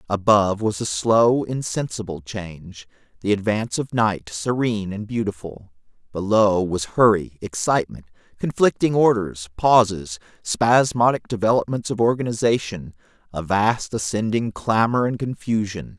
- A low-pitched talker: Yes, low, 105 Hz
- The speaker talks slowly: Yes, slow, 115 wpm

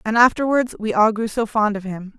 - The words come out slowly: No, fast, 245 wpm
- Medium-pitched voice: No, high, 220 Hz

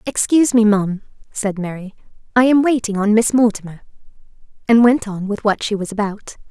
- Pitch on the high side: Yes, high, 215 Hz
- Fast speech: No, average, 175 wpm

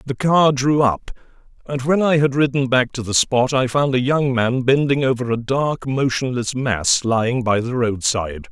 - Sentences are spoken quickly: No, average, 195 wpm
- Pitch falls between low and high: No, low, 130 Hz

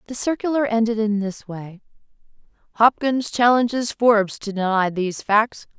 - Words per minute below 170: Yes, slow, 135 wpm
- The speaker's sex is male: No, female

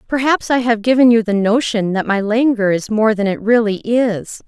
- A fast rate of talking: Yes, fast, 215 wpm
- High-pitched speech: Yes, high, 220 Hz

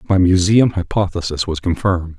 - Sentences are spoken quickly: No, slow, 135 wpm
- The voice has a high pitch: No, very low, 90 Hz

